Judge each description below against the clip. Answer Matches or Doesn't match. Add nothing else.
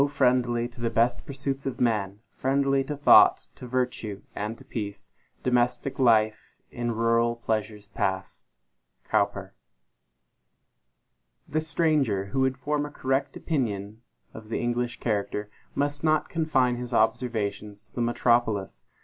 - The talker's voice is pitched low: Matches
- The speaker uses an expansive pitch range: Doesn't match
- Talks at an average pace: Doesn't match